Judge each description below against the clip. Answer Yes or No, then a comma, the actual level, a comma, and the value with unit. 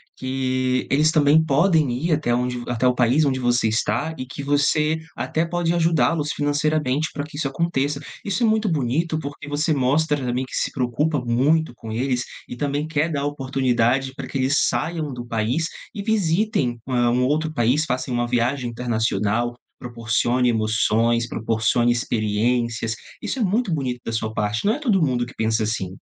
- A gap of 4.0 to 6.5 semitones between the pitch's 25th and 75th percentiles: Yes, average, 4.4 semitones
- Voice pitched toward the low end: Yes, low, 130 Hz